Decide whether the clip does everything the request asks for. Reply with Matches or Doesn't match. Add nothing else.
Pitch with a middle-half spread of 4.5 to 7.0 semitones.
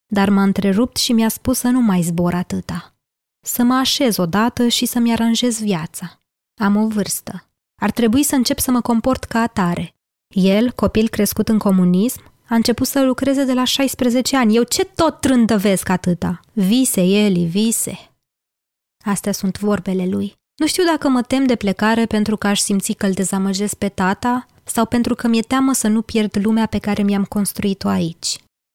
Doesn't match